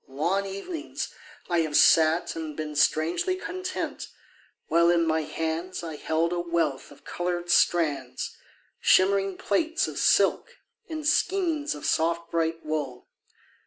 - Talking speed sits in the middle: No, slow, 130 wpm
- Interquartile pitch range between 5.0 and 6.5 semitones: No, average, 3.8 semitones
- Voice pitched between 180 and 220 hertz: No, medium, 170 Hz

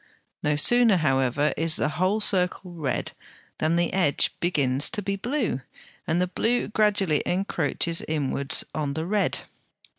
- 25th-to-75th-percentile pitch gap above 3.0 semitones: Yes, average, 5.0 semitones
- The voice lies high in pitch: No, medium, 170 Hz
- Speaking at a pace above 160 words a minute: No, average, 145 wpm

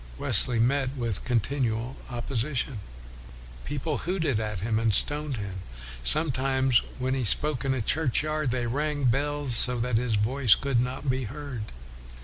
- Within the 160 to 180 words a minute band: No, average, 150 wpm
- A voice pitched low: Yes, low, 130 Hz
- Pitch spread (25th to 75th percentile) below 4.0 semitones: Yes, average, 3.4 semitones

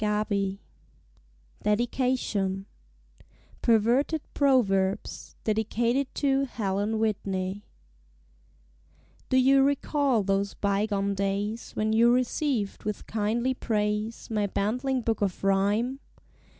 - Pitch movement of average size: Yes, average, 3.8 semitones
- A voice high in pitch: Yes, high, 215 Hz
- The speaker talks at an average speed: No, slow, 90 wpm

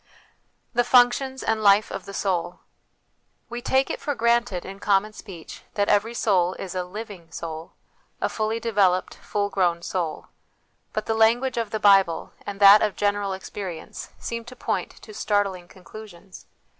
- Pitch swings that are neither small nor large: Yes, average, 3.4 semitones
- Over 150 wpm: Yes, average, 165 wpm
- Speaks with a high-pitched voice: Yes, high, 205 Hz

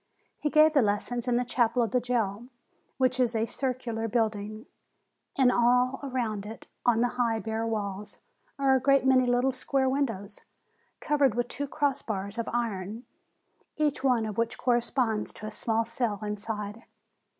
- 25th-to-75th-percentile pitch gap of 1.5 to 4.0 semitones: Yes, average, 2.8 semitones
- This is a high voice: Yes, high, 240 Hz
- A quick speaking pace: No, average, 170 wpm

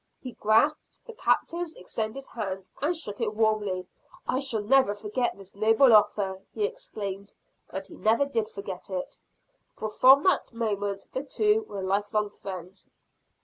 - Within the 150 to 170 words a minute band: Yes, average, 155 wpm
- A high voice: Yes, high, 215 Hz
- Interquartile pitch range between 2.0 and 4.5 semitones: No, average, 5.3 semitones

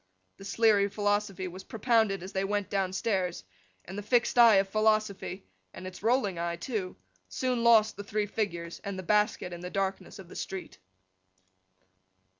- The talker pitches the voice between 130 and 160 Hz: No, high, 195 Hz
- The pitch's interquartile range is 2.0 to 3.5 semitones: Yes, narrow, 2.6 semitones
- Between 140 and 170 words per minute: Yes, average, 155 wpm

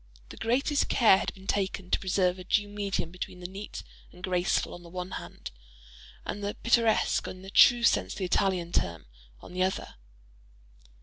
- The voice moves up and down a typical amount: No, narrow, 2.3 semitones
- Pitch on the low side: No, high, 190 Hz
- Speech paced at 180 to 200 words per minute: Yes, average, 185 wpm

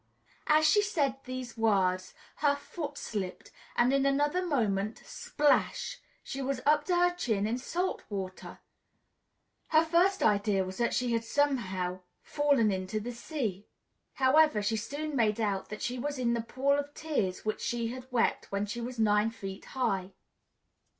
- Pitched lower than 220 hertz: No, high, 240 Hz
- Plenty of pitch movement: Yes, wide, 5.7 semitones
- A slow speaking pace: No, average, 165 wpm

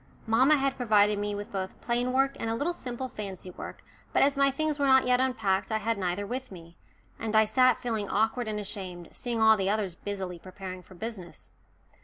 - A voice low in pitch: No, high, 220 Hz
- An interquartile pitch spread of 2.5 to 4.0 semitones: No, average, 4.5 semitones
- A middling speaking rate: No, fast, 210 wpm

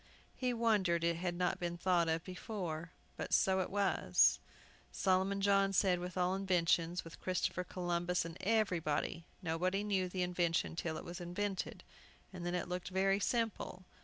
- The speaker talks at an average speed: Yes, average, 160 wpm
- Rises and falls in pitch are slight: Yes, narrow, 2.1 semitones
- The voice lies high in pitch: No, medium, 180 Hz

